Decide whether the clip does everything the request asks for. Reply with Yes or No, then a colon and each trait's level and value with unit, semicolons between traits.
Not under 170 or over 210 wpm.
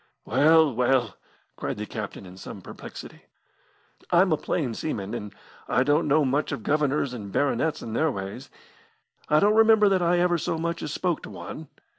Yes: average, 180 wpm